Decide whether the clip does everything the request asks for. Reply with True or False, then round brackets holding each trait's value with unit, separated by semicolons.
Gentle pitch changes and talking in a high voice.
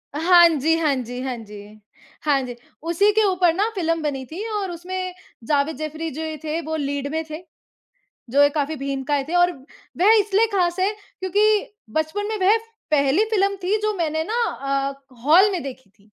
False (5.0 semitones; 320 Hz)